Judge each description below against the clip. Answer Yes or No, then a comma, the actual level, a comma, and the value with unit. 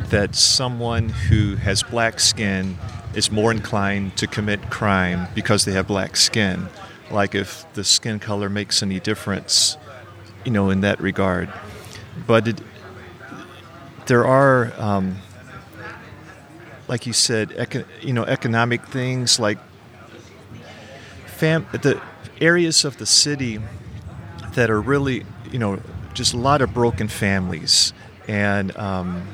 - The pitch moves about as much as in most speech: Yes, average, 3.1 semitones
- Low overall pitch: Yes, low, 110 Hz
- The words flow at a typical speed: No, slow, 130 wpm